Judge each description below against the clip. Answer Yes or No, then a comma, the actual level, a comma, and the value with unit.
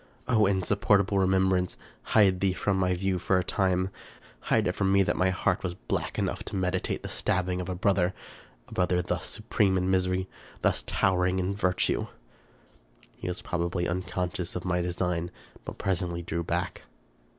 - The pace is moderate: Yes, average, 175 wpm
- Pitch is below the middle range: Yes, very low, 90 Hz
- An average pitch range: No, narrow, 1.2 semitones